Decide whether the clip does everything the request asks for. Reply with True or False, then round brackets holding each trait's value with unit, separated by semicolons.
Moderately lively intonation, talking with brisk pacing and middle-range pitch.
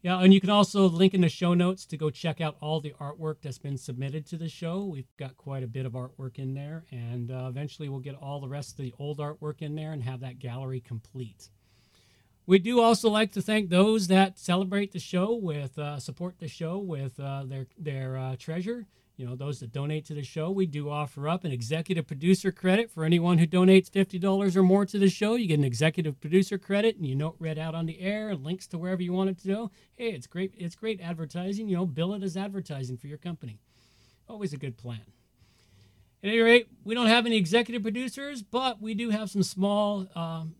False (5.8 semitones; 230 wpm; 165 Hz)